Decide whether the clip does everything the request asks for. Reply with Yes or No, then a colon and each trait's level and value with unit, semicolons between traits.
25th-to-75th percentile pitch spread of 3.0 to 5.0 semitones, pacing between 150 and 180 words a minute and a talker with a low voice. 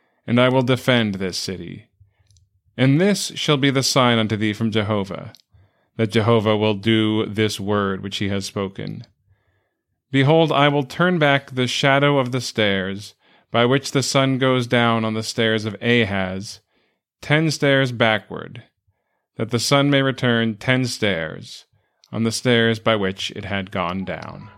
Yes: average, 4.6 semitones; average, 160 wpm; low, 115 Hz